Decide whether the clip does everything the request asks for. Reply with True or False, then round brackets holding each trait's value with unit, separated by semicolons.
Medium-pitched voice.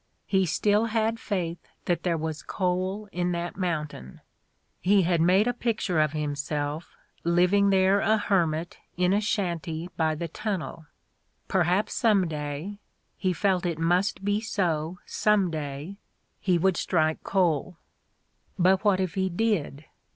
True (180 Hz)